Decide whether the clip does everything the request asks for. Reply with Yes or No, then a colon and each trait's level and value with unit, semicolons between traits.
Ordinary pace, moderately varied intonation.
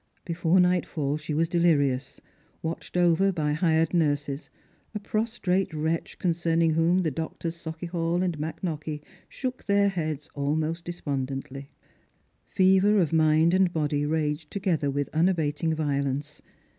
No: slow, 130 wpm; average, 3.0 semitones